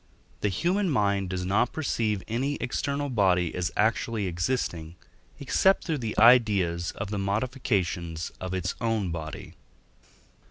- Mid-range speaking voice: No, low, 105 Hz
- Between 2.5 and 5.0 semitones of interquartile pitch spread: No, wide, 5.4 semitones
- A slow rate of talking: Yes, slow, 130 wpm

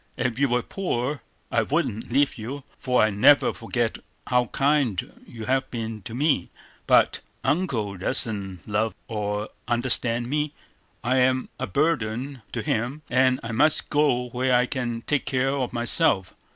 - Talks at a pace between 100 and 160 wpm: Yes, average, 155 wpm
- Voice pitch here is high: No, low, 125 Hz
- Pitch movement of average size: Yes, average, 3.2 semitones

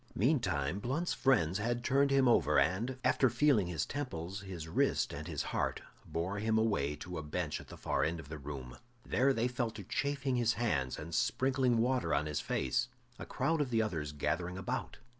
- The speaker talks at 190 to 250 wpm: Yes, average, 195 wpm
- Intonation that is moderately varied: No, wide, 7.9 semitones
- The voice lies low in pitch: Yes, low, 105 Hz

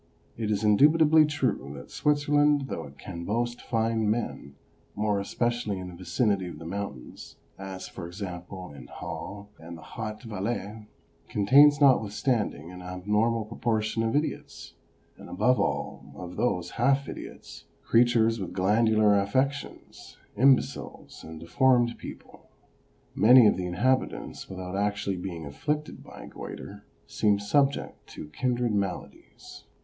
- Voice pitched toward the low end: Yes, low, 105 Hz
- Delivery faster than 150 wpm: No, slow, 135 wpm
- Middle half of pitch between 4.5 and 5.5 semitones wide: Yes, average, 4.9 semitones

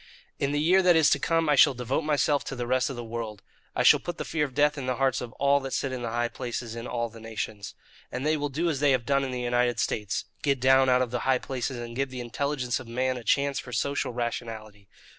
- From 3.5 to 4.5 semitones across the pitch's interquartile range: No, average, 2.9 semitones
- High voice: No, low, 130 Hz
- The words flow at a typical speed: No, fast, 275 wpm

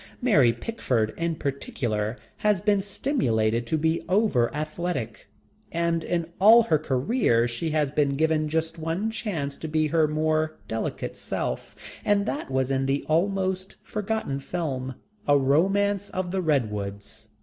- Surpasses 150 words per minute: No, average, 145 wpm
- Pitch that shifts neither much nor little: No, wide, 5.9 semitones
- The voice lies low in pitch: No, medium, 155 Hz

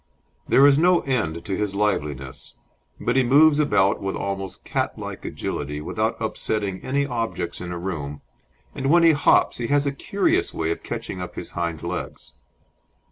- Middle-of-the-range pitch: No, low, 100 Hz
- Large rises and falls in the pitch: Yes, wide, 8.4 semitones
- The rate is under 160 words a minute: No, average, 170 wpm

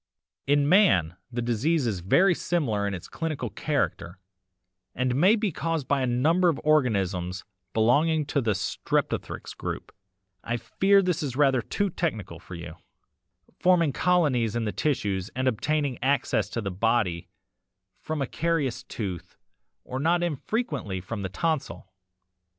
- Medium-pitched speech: No, low, 130 Hz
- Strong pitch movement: Yes, wide, 7.6 semitones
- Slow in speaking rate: No, average, 145 wpm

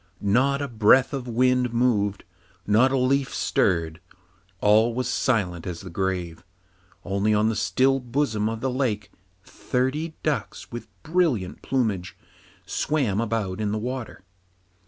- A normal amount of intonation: Yes, average, 4.2 semitones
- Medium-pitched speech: No, low, 115 Hz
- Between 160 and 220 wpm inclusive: No, slow, 135 wpm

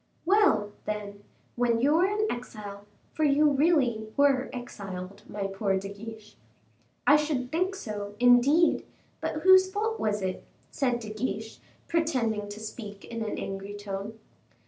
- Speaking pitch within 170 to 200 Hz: No, high, 225 Hz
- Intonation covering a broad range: Yes, wide, 6.3 semitones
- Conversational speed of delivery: Yes, average, 150 wpm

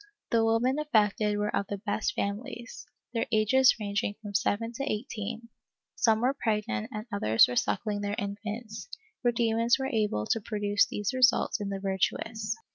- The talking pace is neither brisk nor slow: Yes, average, 170 wpm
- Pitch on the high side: Yes, high, 215 Hz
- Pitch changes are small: Yes, narrow, 2.3 semitones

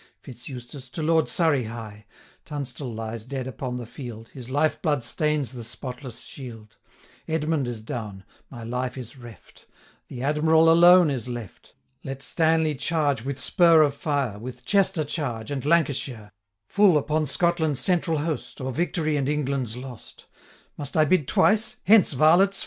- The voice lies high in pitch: No, medium, 140 Hz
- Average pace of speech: Yes, average, 160 wpm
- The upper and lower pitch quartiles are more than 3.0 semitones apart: Yes, average, 4.4 semitones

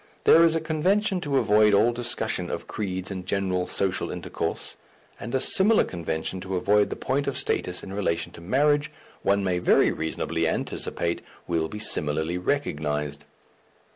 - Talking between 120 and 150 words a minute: No, average, 160 wpm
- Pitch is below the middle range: Yes, low, 100 Hz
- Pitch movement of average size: No, wide, 8.2 semitones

